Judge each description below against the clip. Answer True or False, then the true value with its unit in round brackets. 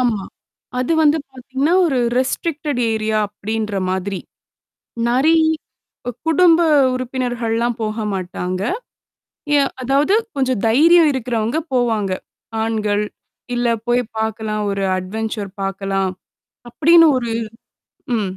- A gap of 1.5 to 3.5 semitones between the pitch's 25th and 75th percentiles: False (3.9 semitones)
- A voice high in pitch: True (235 Hz)